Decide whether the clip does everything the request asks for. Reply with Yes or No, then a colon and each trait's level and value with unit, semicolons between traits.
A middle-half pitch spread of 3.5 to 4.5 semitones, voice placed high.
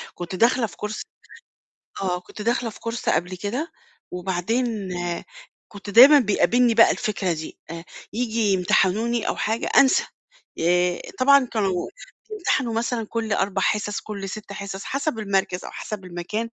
Yes: average, 3.9 semitones; high, 210 Hz